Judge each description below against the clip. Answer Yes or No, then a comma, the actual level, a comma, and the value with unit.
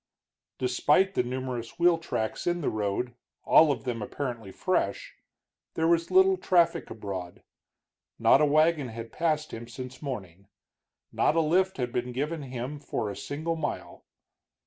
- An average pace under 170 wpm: Yes, average, 150 wpm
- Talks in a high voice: No, low, 130 Hz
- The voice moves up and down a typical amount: No, wide, 5.8 semitones